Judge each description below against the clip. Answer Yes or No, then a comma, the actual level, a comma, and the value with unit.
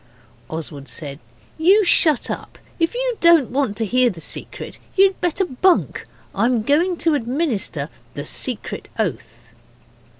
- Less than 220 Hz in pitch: No, very high, 255 Hz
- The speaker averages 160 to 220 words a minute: No, slow, 135 wpm